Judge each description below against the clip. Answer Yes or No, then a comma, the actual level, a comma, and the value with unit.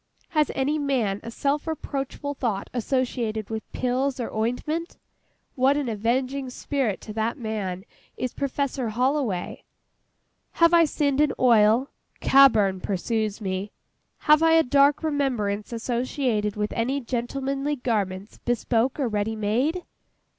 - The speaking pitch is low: No, very high, 250 Hz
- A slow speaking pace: Yes, slow, 130 wpm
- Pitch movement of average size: Yes, average, 4.3 semitones